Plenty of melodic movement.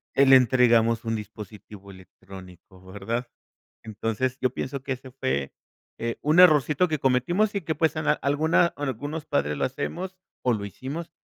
Yes: wide, 5.8 semitones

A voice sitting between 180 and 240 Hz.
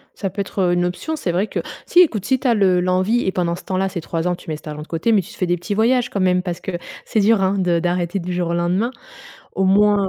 Yes: medium, 185 Hz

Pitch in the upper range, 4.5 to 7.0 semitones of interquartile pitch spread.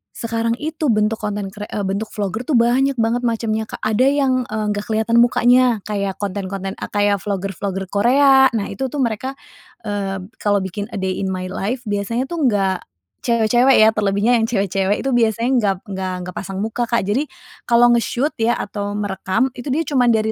No: high, 215 Hz; average, 3.3 semitones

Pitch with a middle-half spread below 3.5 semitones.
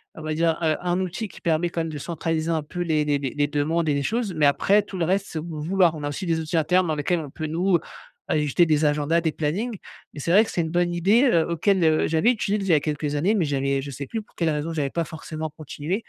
Yes: average, 2.9 semitones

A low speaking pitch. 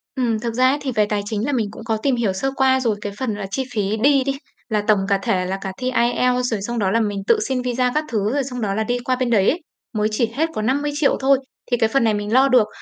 No: high, 235 Hz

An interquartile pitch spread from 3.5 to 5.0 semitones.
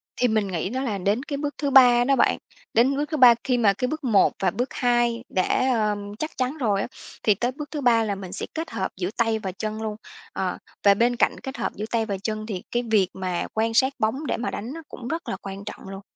Yes: average, 4.2 semitones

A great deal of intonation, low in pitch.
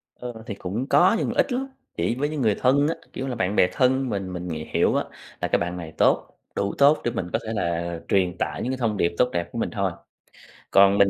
Yes: wide, 6.4 semitones; low, 105 Hz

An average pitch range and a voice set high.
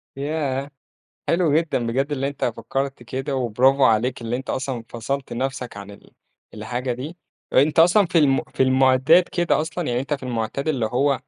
No: average, 3.0 semitones; low, 135 Hz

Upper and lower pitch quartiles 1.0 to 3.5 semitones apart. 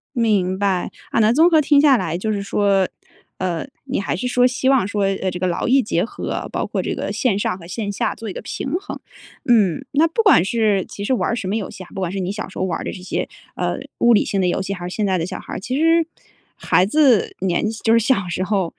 No: average, 4.8 semitones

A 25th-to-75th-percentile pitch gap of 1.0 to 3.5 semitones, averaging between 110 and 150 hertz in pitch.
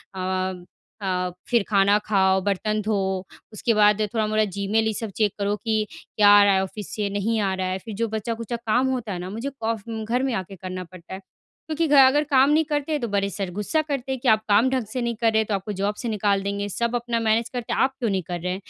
No: average, 3.2 semitones; high, 215 Hz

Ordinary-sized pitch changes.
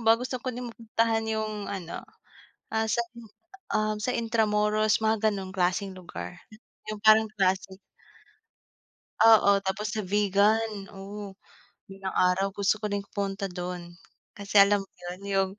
No: narrow, 2.2 semitones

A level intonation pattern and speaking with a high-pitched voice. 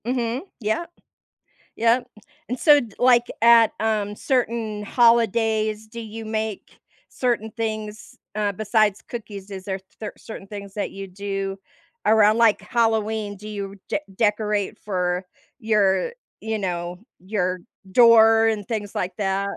Yes: narrow, 2.2 semitones; high, 215 Hz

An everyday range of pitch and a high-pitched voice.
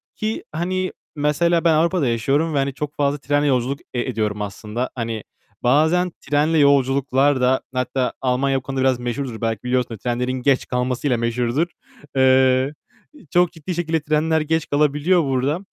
No: average, 3.5 semitones; low, 135 Hz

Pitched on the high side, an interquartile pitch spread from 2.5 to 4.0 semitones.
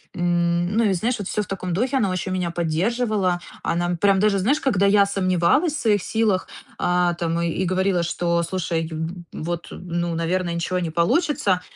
No: medium, 180 Hz; average, 2.8 semitones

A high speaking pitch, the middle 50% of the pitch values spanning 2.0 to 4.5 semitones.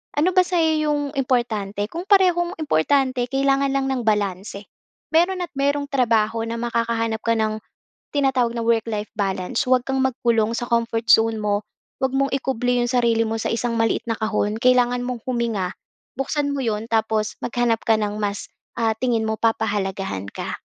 Yes: high, 235 Hz; average, 3.5 semitones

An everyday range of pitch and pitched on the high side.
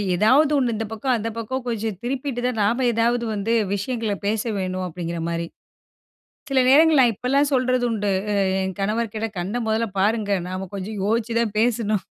Yes: average, 3.4 semitones; high, 225 Hz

